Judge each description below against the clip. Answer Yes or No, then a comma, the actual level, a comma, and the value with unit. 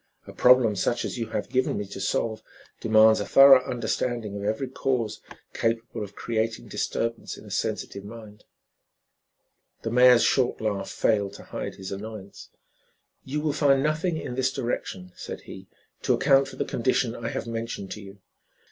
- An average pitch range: Yes, average, 3.4 semitones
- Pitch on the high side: No, low, 115 Hz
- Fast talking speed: No, average, 170 wpm